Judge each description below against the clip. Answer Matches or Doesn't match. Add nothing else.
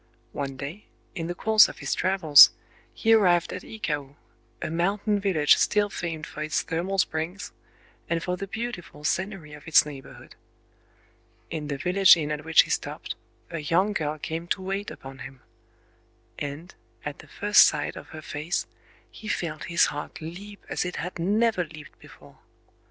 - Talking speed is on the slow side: Doesn't match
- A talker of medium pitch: Matches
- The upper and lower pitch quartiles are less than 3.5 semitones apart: Doesn't match